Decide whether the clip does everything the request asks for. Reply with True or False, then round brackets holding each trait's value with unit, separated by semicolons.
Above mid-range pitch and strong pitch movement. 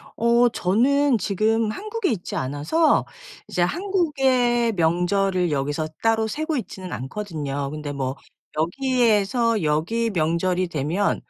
True (205 Hz; 7.0 semitones)